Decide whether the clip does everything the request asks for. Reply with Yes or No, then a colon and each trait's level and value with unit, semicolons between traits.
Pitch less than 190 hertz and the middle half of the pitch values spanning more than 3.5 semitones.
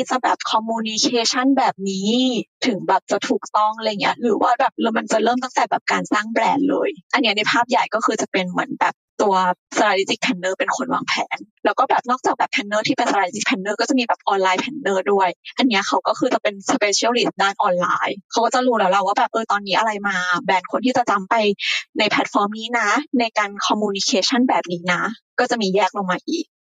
No: high, 220 Hz; average, 4.1 semitones